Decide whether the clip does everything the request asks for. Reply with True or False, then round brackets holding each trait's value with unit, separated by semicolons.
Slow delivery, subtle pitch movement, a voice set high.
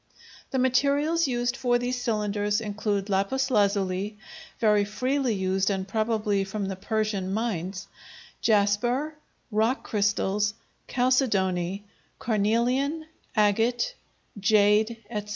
False (100 wpm; 3.4 semitones; 215 Hz)